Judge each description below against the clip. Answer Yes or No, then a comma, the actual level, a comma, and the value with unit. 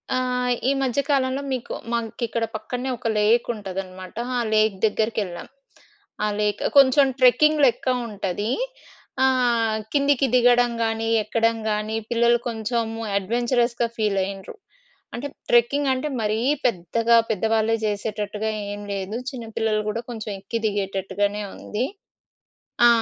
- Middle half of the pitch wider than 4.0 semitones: No, narrow, 2.6 semitones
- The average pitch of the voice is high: Yes, high, 225 Hz